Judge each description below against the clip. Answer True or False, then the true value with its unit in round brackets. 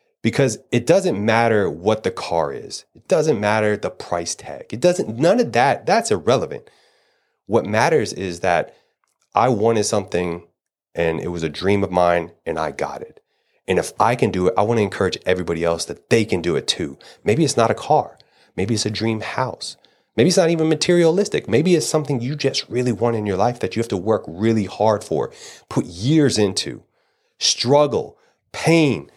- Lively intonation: True (7.6 semitones)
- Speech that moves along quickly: False (195 wpm)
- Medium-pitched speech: False (115 Hz)